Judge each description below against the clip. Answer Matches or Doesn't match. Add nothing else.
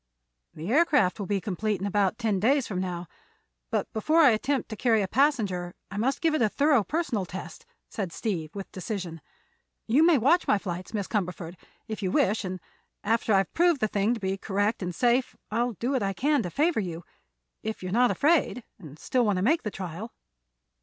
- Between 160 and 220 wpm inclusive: Matches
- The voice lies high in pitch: Matches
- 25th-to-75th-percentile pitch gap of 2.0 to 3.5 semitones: Doesn't match